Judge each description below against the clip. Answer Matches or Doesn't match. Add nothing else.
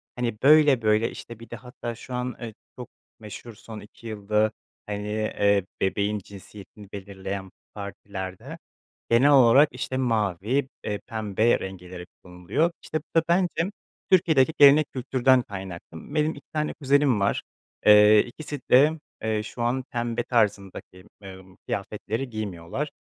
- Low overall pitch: Matches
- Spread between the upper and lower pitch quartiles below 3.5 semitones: Doesn't match